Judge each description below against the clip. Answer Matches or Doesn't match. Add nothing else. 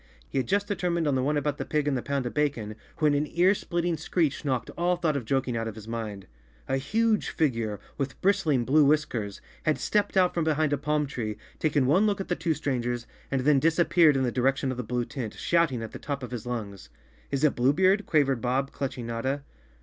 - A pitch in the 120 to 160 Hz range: Matches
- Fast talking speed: Matches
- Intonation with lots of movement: Doesn't match